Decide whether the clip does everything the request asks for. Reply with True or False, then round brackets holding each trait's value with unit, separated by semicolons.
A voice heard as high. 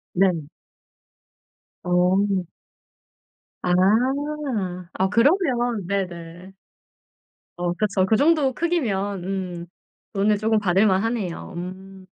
True (195 Hz)